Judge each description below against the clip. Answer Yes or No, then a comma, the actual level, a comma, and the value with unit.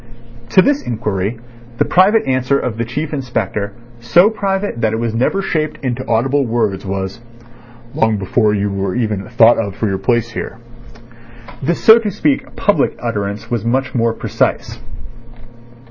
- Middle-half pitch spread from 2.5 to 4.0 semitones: No, average, 4.6 semitones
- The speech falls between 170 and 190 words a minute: No, average, 160 wpm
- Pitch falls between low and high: No, low, 120 Hz